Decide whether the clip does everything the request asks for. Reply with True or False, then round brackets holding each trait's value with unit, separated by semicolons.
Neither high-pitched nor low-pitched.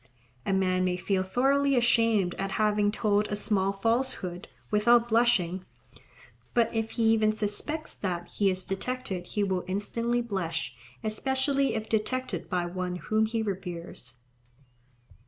False (210 Hz)